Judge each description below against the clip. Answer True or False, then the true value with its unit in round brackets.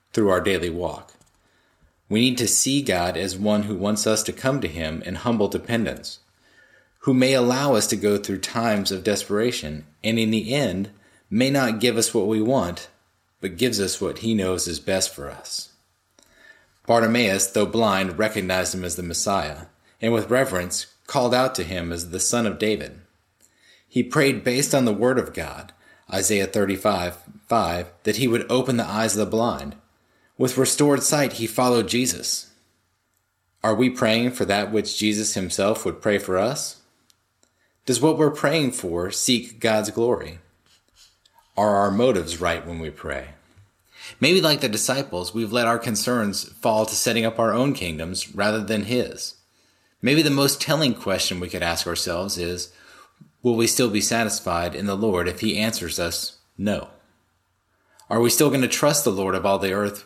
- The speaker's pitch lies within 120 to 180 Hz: False (105 Hz)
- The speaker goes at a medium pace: True (180 wpm)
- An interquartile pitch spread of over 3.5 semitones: True (4.3 semitones)